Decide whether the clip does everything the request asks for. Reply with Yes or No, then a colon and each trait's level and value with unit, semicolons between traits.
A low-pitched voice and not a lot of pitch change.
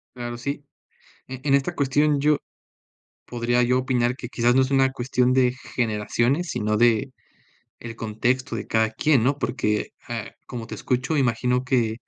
Yes: low, 125 Hz; narrow, 2.2 semitones